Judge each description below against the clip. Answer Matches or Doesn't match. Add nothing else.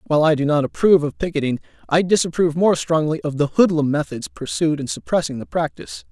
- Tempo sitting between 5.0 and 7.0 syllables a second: Matches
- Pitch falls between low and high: Matches